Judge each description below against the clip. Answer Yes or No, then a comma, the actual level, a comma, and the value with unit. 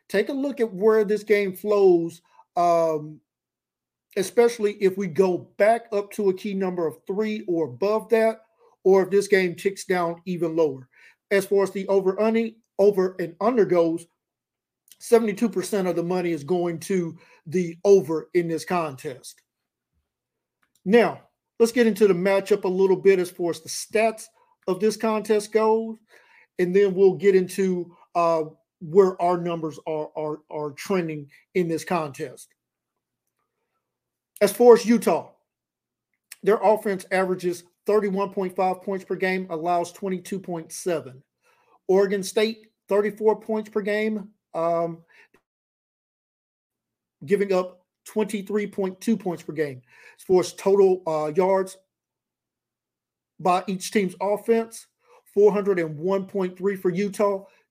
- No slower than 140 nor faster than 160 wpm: Yes, average, 150 wpm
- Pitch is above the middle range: Yes, high, 195 Hz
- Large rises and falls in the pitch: No, average, 3.3 semitones